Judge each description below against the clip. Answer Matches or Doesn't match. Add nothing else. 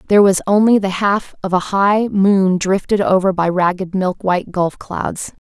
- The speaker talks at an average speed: Matches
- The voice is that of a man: Doesn't match